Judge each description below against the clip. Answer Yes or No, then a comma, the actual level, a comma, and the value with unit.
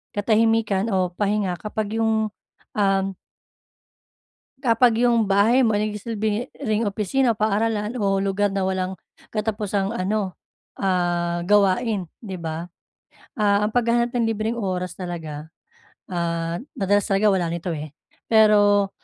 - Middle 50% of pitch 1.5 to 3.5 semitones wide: Yes, average, 2.8 semitones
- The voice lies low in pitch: No, high, 205 Hz